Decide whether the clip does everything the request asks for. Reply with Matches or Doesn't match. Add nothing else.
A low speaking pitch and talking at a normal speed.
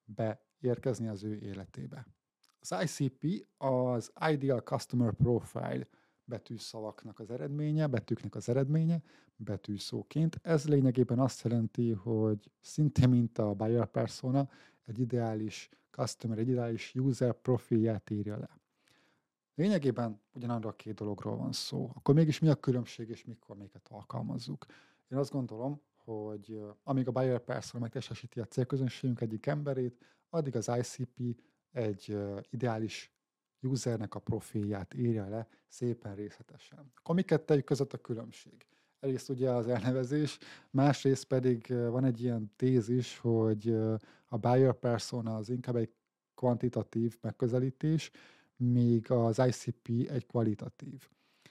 Matches